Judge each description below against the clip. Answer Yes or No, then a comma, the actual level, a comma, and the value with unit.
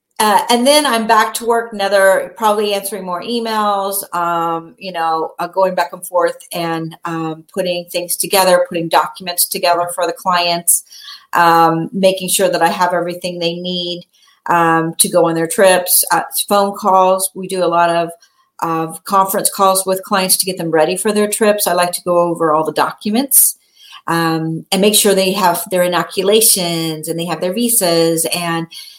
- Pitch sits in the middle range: Yes, medium, 180 Hz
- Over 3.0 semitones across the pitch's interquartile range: No, average, 2.7 semitones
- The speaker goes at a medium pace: Yes, average, 180 wpm